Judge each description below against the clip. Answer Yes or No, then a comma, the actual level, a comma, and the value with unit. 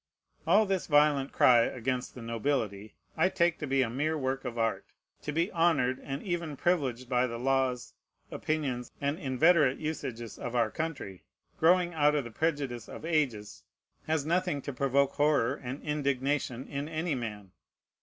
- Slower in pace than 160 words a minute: No, average, 165 wpm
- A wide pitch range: No, average, 4.0 semitones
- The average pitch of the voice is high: No, medium, 140 Hz